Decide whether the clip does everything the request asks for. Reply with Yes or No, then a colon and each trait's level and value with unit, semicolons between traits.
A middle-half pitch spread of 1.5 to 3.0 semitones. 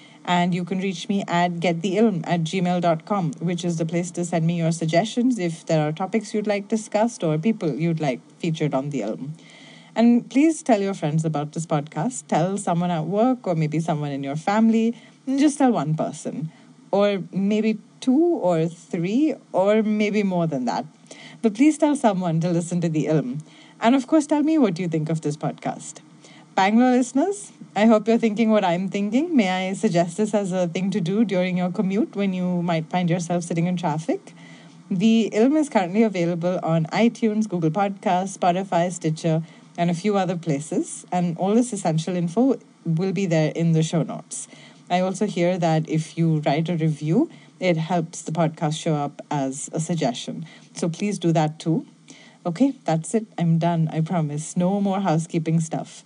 No: average, 4.6 semitones